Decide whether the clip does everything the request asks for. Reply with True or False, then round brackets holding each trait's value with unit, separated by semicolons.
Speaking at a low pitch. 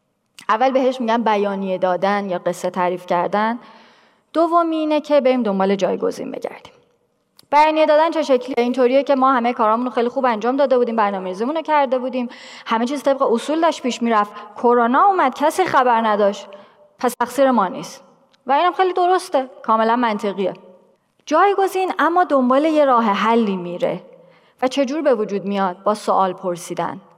False (245 Hz)